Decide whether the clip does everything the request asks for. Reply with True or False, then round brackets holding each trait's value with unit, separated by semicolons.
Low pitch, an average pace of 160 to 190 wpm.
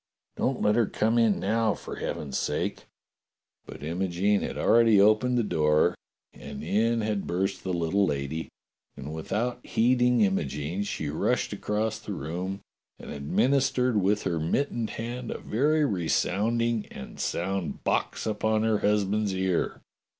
False (105 Hz; 145 wpm)